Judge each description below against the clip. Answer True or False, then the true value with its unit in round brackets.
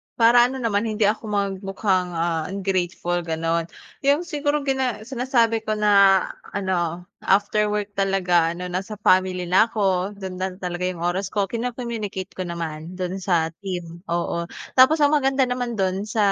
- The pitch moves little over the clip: False (4.1 semitones)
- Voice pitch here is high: True (195 Hz)